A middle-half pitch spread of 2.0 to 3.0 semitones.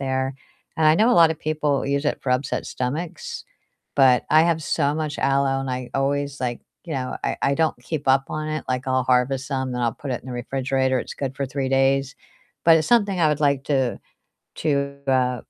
Yes: narrow, 2.5 semitones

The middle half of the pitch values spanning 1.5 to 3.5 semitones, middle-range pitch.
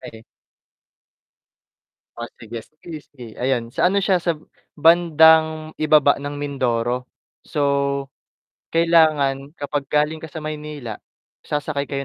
Yes: average, 2.7 semitones; medium, 150 Hz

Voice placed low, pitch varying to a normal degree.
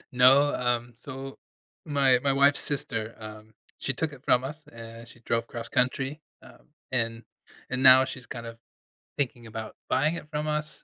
Yes: low, 130 Hz; average, 3.4 semitones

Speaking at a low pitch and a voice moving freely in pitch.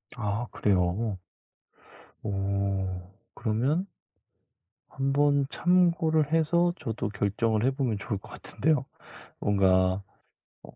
Yes: low, 110 Hz; wide, 6.8 semitones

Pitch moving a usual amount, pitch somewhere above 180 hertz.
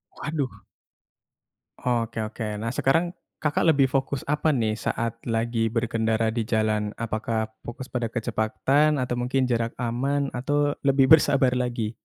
No: average, 3.4 semitones; low, 120 Hz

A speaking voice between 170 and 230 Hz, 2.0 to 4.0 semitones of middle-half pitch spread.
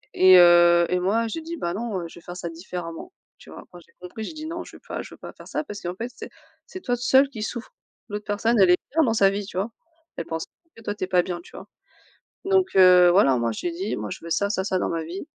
No: high, 190 Hz; average, 4.7 semitones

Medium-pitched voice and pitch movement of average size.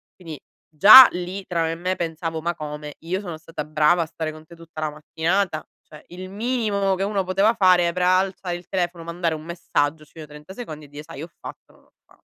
Yes: medium, 170 Hz; average, 3.0 semitones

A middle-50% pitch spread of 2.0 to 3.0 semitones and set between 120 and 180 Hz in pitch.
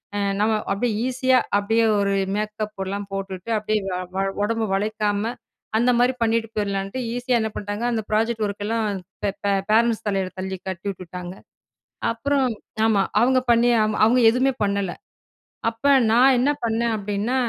No: average, 2.7 semitones; high, 215 Hz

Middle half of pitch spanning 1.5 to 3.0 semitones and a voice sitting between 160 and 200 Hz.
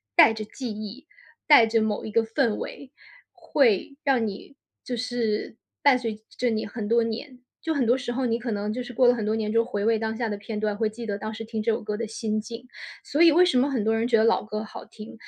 No: narrow, 2.4 semitones; high, 225 Hz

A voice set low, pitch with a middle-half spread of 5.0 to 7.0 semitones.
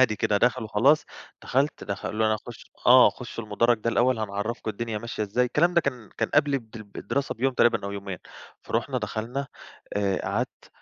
No: low, 115 Hz; average, 3.2 semitones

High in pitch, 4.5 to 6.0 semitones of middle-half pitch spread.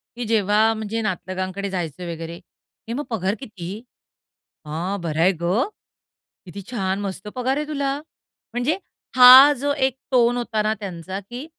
Yes: high, 205 Hz; average, 4.8 semitones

